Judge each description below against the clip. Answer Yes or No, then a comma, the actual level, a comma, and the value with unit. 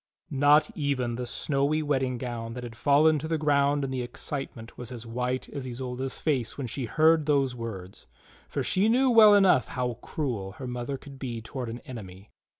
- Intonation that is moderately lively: Yes, average, 3.4 semitones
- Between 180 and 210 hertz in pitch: No, low, 130 Hz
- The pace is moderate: Yes, average, 190 wpm